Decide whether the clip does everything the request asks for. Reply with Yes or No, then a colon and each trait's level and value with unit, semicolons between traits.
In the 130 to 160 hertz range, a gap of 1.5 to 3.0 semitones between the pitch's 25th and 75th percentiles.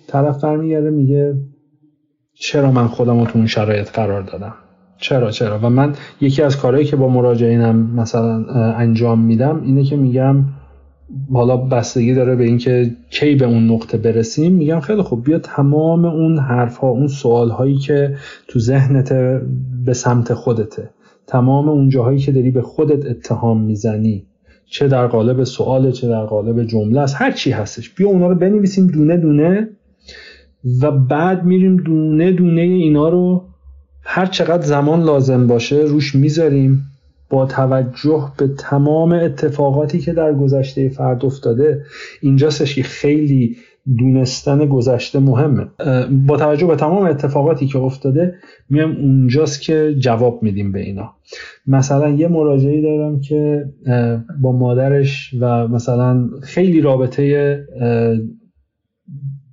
No: low, 135 Hz; average, 3.6 semitones